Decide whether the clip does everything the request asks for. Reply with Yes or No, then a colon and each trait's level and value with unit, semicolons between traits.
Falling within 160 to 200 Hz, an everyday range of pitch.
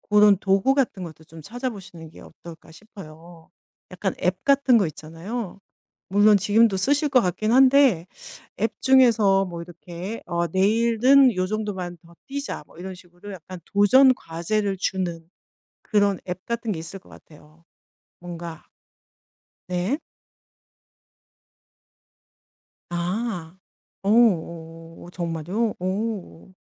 Yes: high, 190 Hz; average, 4.7 semitones